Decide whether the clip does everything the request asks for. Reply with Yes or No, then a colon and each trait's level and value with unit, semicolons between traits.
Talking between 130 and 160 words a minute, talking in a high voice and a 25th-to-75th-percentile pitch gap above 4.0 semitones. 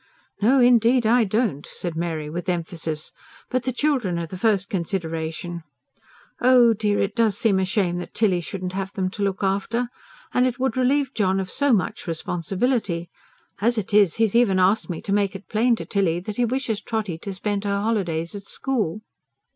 No: average, 190 wpm; high, 200 Hz; average, 4.5 semitones